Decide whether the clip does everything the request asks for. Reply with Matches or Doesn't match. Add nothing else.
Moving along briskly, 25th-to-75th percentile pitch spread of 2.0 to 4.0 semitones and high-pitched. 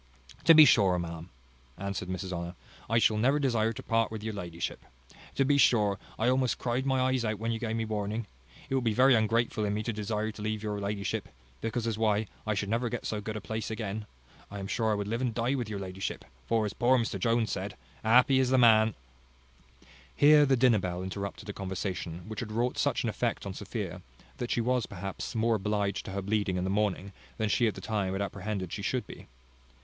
Doesn't match